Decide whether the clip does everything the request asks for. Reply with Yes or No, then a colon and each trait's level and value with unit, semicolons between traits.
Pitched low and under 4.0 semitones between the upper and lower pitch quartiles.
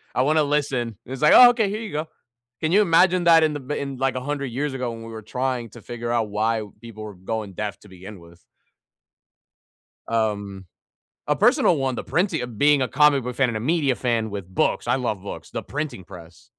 No: low, 125 Hz; wide, 5.4 semitones